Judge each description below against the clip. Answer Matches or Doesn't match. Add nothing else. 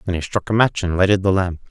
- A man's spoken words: Matches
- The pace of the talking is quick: Matches